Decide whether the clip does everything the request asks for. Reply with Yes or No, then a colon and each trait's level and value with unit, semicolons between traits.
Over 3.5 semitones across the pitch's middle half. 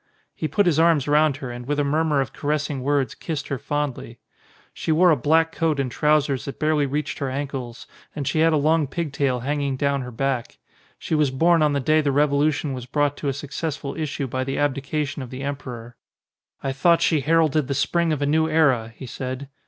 No: narrow, 2.4 semitones